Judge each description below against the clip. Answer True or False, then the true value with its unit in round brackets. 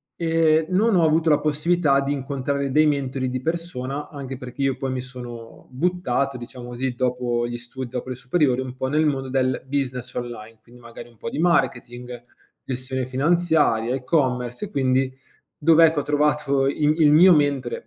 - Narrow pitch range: False (3.1 semitones)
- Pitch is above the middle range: False (135 Hz)